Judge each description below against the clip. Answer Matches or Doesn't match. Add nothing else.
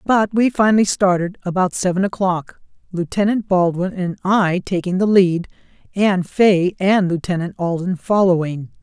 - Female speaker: Matches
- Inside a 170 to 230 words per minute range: Doesn't match